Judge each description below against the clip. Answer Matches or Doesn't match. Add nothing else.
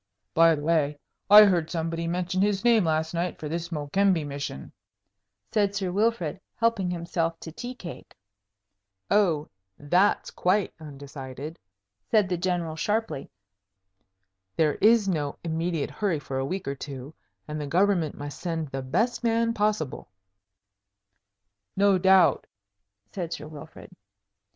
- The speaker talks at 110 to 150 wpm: Matches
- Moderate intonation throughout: Matches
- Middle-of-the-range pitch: Matches